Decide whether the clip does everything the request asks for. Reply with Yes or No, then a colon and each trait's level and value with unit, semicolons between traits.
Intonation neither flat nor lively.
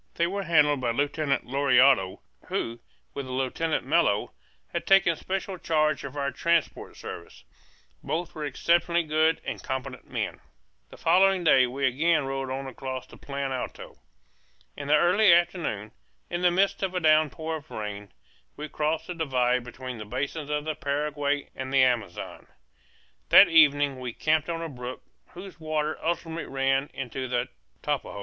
Yes: average, 3.9 semitones